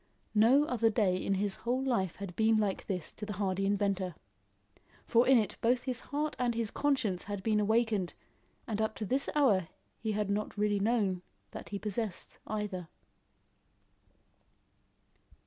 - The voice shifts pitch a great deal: No, average, 3.0 semitones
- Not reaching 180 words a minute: Yes, average, 160 wpm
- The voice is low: No, high, 210 Hz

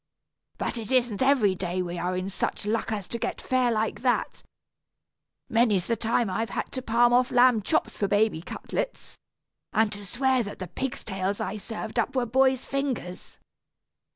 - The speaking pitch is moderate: No, high, 225 Hz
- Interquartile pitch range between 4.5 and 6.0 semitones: No, average, 4.0 semitones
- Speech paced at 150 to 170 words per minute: No, average, 180 wpm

